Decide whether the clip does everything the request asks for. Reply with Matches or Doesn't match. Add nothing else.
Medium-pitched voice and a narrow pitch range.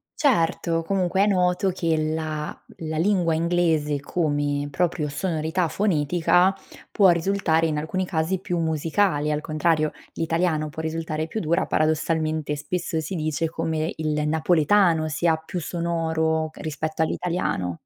Matches